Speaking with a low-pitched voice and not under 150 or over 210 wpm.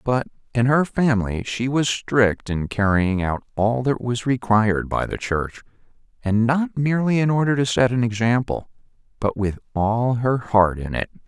Yes: low, 120 Hz; average, 170 wpm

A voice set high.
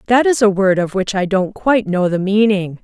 Yes: high, 200 Hz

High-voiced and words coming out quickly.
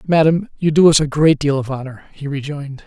No: medium, 145 Hz; fast, 230 wpm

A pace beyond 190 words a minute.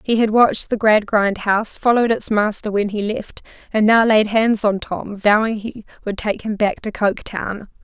Yes: average, 200 wpm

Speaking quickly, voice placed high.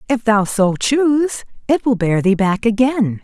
No: average, 185 wpm; high, 230 Hz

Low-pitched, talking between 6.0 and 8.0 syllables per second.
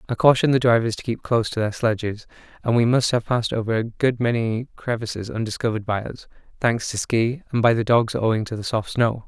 Yes: low, 115 Hz; 6.1 syllables/s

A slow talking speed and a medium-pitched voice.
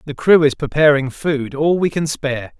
No: fast, 210 wpm; medium, 145 Hz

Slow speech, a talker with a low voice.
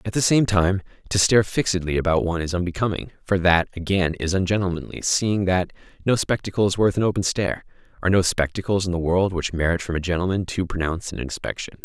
No: average, 200 wpm; very low, 90 Hz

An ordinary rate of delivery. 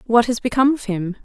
No: fast, 240 wpm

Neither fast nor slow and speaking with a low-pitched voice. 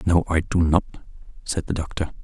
Yes: average, 190 wpm; very low, 85 Hz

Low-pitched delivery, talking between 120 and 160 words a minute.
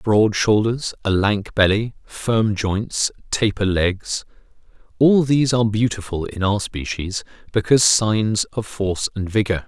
Yes: low, 105 Hz; slow, 135 wpm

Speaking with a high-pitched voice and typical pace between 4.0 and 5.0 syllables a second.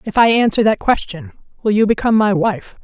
No: high, 215 Hz; 5.8 syllables/s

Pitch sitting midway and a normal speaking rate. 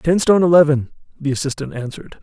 Yes: medium, 150 Hz; average, 160 wpm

